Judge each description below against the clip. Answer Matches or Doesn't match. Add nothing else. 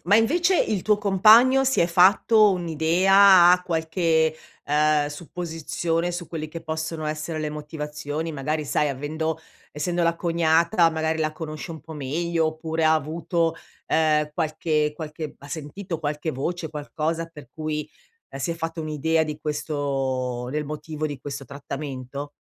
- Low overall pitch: Doesn't match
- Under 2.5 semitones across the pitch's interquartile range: Matches